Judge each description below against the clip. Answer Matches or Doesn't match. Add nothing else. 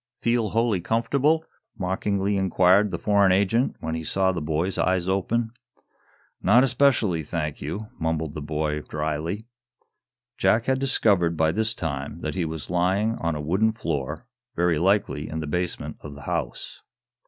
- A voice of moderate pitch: Doesn't match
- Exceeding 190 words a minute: Doesn't match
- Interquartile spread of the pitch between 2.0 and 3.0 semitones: Doesn't match